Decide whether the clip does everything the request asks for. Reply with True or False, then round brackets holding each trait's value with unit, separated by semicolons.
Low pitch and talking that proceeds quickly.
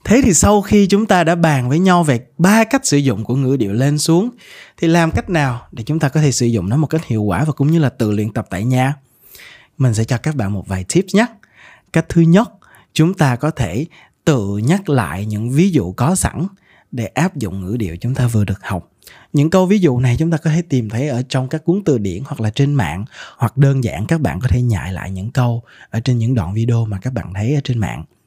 True (130 Hz; 260 wpm)